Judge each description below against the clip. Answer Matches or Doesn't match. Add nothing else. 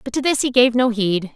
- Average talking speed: Doesn't match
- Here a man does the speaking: Doesn't match